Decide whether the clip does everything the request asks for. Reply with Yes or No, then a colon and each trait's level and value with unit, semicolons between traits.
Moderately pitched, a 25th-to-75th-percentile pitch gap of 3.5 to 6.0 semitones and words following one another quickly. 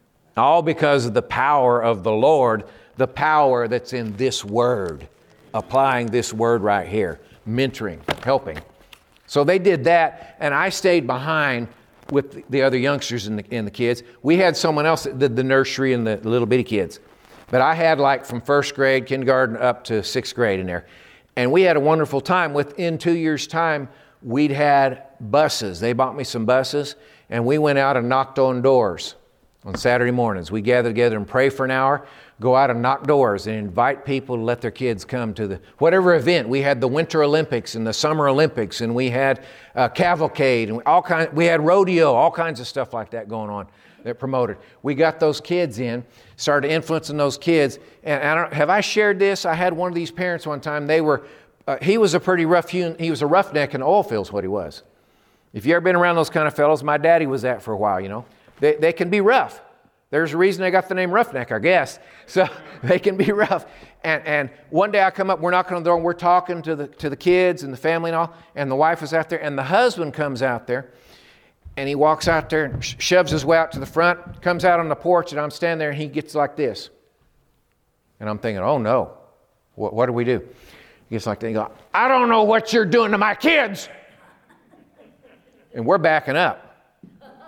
Yes: medium, 145 Hz; average, 5.2 semitones; fast, 225 wpm